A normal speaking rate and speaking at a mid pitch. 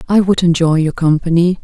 Yes: average, 185 wpm; medium, 170 Hz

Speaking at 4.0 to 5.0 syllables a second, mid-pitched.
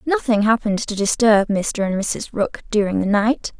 No: 4.7 syllables/s; high, 215 Hz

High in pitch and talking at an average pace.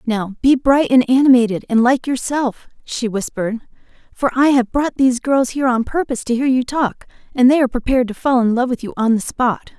No: very high, 250 Hz; fast, 220 wpm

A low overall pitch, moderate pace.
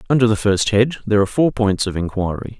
No: low, 110 Hz; fast, 230 wpm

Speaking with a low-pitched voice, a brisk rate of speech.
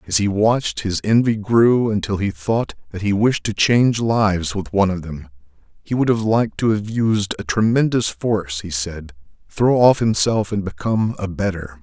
No: low, 105 Hz; average, 195 wpm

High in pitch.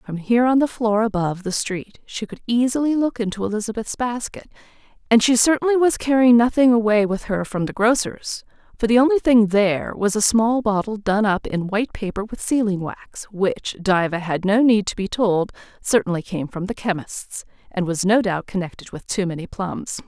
Yes: high, 215 Hz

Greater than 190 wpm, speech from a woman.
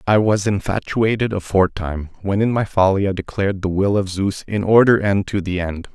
No: average, 200 wpm; male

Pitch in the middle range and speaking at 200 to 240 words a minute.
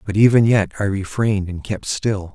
No: low, 100 Hz; fast, 205 wpm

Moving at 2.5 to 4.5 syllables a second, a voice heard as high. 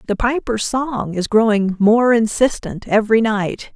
Yes: 4.2 syllables/s; high, 225 Hz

